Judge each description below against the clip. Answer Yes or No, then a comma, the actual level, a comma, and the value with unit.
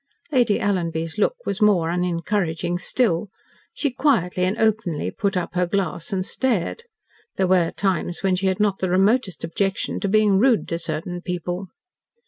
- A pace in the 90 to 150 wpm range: No, average, 160 wpm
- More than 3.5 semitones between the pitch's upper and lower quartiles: No, average, 3.1 semitones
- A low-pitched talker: No, high, 190 Hz